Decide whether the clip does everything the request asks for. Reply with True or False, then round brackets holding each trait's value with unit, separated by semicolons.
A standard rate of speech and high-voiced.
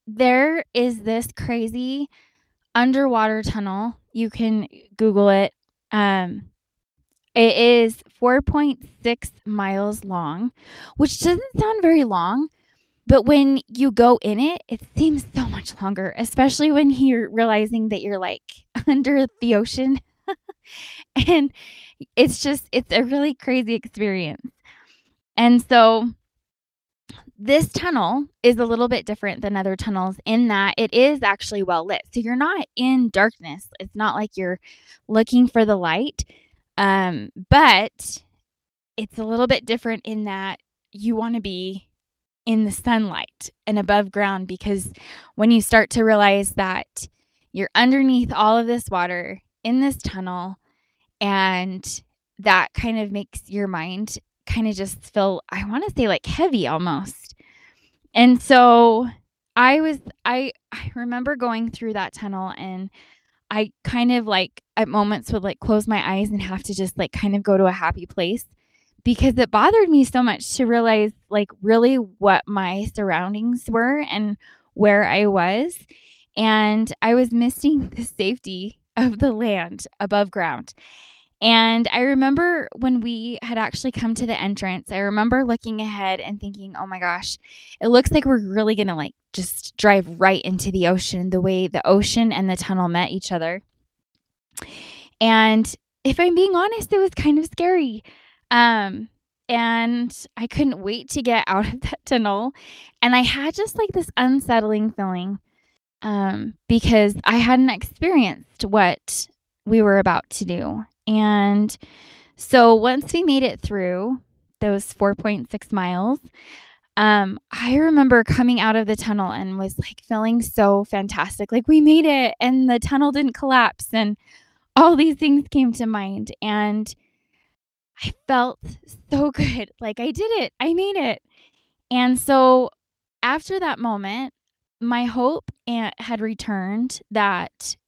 True (150 wpm; 225 Hz)